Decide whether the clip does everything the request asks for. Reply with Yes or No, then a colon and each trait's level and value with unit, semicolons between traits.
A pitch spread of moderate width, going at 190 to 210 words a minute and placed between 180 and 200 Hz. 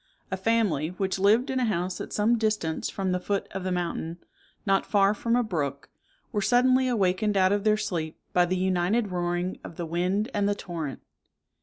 Yes: average, 3.2 semitones; average, 195 wpm; high, 190 Hz